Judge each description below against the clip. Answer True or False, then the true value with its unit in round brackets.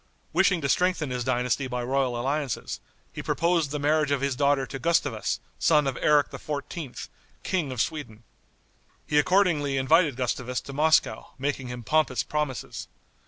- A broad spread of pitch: False (3.0 semitones)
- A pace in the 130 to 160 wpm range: True (155 wpm)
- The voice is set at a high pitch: False (140 Hz)